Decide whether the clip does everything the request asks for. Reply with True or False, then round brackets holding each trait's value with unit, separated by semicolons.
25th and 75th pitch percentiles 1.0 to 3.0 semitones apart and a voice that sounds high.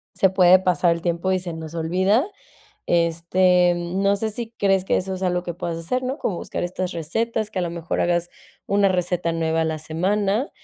False (2.4 semitones; 180 Hz)